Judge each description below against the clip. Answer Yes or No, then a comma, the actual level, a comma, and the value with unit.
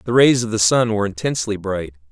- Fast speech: Yes, fast, 225 wpm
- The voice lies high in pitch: No, low, 105 Hz